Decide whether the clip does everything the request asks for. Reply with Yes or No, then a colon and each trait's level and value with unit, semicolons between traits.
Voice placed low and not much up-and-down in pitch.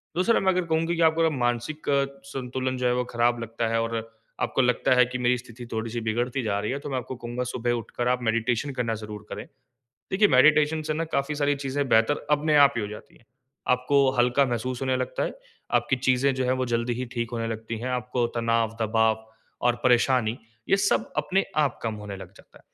No: low, 125 Hz; average, 3.2 semitones